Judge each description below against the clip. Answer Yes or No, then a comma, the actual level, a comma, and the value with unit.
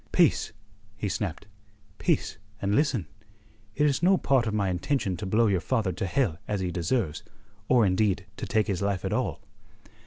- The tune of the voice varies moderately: Yes, average, 4.5 semitones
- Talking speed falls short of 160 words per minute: No, average, 180 wpm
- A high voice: No, low, 100 Hz